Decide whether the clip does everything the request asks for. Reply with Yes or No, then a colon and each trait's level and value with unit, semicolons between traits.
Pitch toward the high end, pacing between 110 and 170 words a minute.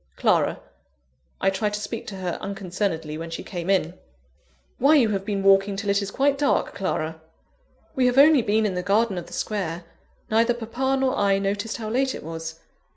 No: high, 200 Hz; average, 195 wpm